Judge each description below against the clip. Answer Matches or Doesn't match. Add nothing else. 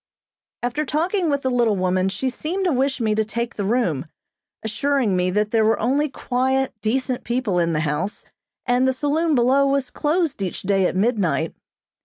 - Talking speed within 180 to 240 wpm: Matches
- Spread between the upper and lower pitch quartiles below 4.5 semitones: Doesn't match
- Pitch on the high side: Matches